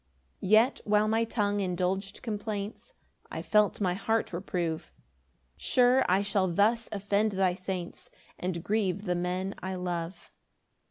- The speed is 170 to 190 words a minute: No, average, 140 wpm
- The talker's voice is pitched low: No, high, 195 Hz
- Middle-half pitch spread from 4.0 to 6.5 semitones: No, average, 2.8 semitones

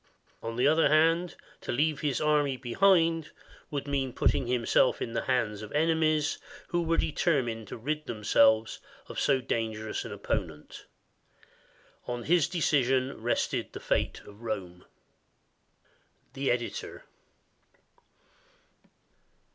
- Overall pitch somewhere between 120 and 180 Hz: Yes, low, 135 Hz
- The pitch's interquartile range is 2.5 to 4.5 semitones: No, average, 5.2 semitones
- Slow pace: Yes, slow, 125 wpm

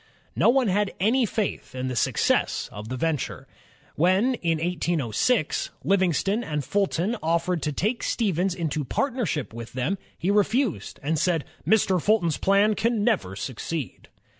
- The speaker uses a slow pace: No, average, 145 wpm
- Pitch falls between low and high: Yes, medium, 180 Hz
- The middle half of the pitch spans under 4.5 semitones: No, wide, 5.6 semitones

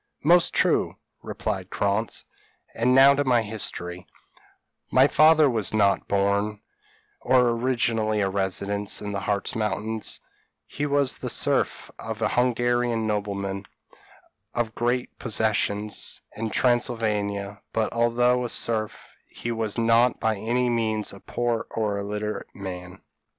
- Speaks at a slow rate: Yes, slow, 130 wpm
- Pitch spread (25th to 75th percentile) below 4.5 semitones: Yes, average, 3.0 semitones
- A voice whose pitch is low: Yes, low, 110 Hz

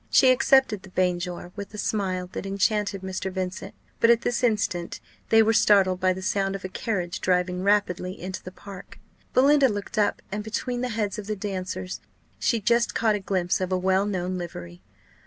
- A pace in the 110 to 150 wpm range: No, average, 195 wpm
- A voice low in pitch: No, high, 195 Hz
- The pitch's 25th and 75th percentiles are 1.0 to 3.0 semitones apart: Yes, narrow, 2.6 semitones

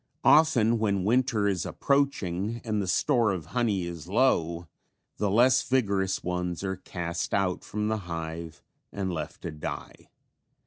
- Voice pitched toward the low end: Yes, low, 100 Hz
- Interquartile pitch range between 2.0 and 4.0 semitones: No, average, 4.7 semitones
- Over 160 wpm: No, average, 145 wpm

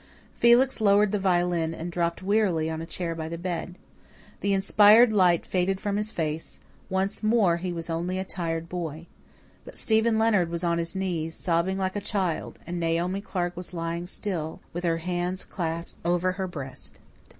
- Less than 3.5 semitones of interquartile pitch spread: Yes, narrow, 2.6 semitones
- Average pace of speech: Yes, average, 180 wpm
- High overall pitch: No, medium, 180 Hz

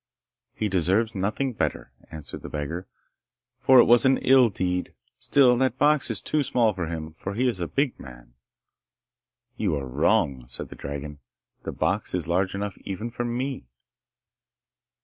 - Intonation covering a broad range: Yes, wide, 7.2 semitones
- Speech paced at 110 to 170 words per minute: Yes, average, 165 wpm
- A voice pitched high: No, low, 100 Hz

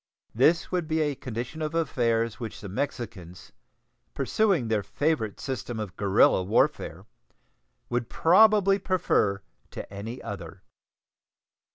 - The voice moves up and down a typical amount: No, wide, 7.7 semitones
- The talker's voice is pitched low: Yes, low, 120 Hz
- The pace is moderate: No, slow, 120 wpm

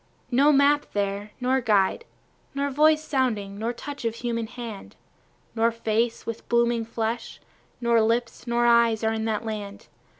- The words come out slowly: No, average, 155 wpm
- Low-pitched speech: No, high, 230 Hz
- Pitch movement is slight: Yes, narrow, 2.0 semitones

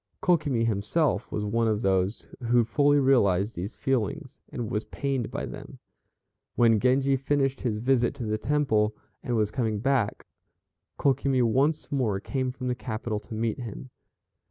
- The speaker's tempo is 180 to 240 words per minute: No, average, 155 wpm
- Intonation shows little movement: No, average, 4.0 semitones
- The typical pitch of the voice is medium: No, low, 120 Hz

